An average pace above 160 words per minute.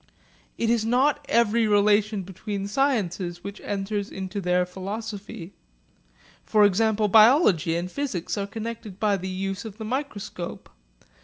No: slow, 135 wpm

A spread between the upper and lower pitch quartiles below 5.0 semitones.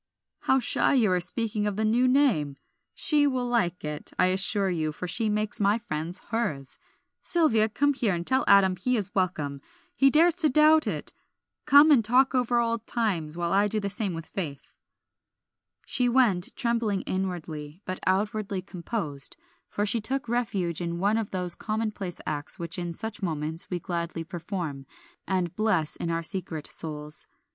No: wide, 5.4 semitones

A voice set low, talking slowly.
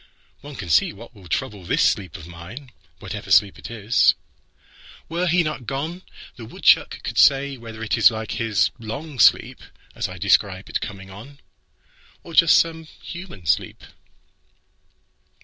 Yes: low, 115 Hz; slow, 130 wpm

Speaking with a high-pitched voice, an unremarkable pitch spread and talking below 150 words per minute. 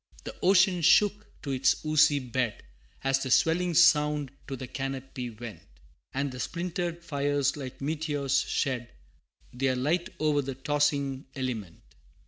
No: medium, 140 Hz; average, 3.2 semitones; slow, 135 wpm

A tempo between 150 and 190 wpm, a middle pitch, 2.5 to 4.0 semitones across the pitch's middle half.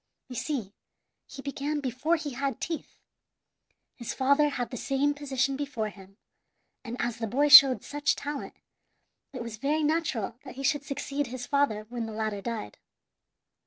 No: average, 160 wpm; very high, 270 Hz; average, 3.7 semitones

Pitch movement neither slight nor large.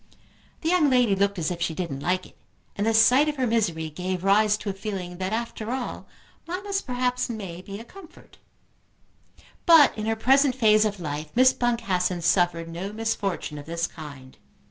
No: wide, 5.9 semitones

